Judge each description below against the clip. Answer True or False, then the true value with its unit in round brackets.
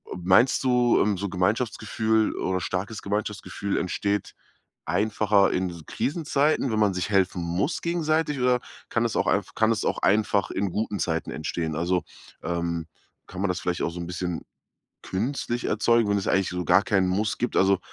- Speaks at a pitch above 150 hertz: False (100 Hz)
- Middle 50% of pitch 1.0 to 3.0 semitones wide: False (3.7 semitones)